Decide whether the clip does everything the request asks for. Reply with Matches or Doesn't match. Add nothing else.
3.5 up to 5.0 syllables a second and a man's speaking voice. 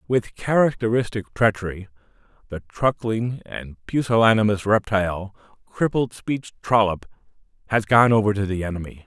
Matches